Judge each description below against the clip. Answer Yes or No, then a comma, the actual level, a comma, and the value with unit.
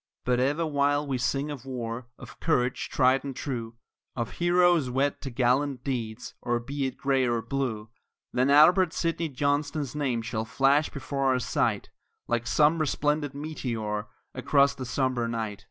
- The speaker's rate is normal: Yes, average, 160 wpm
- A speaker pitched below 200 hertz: Yes, low, 135 Hz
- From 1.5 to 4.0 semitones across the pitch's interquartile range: Yes, average, 3.1 semitones